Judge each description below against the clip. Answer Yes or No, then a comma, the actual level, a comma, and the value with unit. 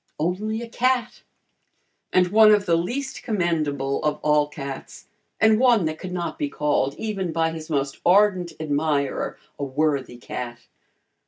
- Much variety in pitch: Yes, wide, 6.4 semitones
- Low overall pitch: No, medium, 170 Hz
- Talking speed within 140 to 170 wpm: Yes, average, 150 wpm